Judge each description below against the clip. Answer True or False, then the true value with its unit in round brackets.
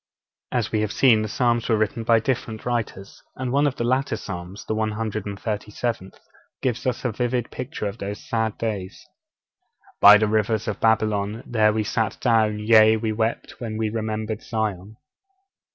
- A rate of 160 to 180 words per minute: True (170 wpm)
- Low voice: True (110 Hz)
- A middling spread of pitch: False (1.7 semitones)